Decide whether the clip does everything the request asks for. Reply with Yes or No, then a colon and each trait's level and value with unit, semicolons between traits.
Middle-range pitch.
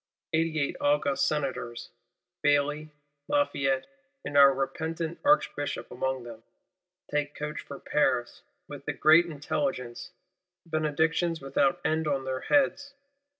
Yes: medium, 150 Hz